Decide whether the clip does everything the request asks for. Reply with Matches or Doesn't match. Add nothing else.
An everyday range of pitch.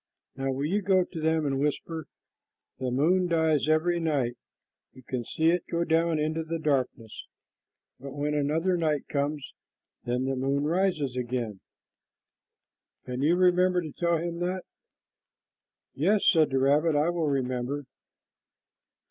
Matches